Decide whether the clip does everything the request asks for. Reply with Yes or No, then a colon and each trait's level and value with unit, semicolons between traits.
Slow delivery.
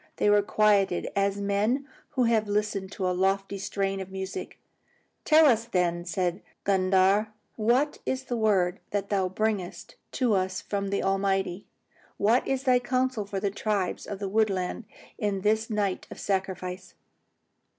No: average, 155 wpm